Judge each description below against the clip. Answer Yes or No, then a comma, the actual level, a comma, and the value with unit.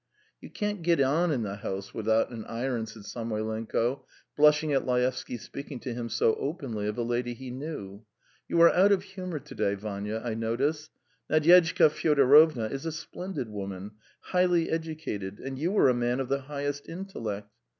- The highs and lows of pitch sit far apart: Yes, wide, 6.0 semitones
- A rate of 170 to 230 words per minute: Yes, average, 175 wpm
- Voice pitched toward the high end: No, low, 130 Hz